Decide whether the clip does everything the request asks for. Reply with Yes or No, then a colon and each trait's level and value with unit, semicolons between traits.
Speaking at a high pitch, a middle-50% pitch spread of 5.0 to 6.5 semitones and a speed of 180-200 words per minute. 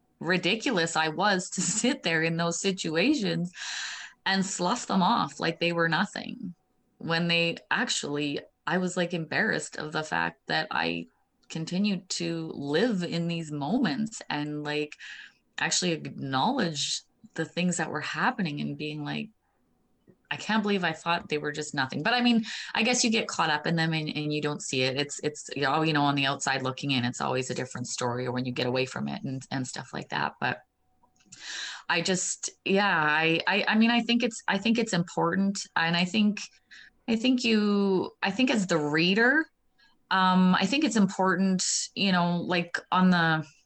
No: medium, 170 Hz; average, 5.3 semitones; average, 190 wpm